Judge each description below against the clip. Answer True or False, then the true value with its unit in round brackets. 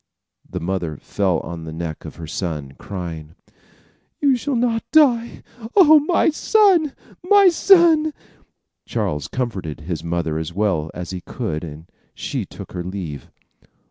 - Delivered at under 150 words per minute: True (140 wpm)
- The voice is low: True (90 Hz)